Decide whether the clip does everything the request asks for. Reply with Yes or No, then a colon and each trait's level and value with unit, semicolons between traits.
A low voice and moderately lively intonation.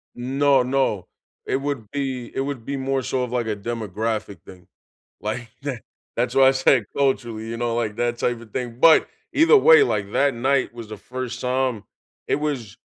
Yes: low, 125 Hz; average, 3.0 semitones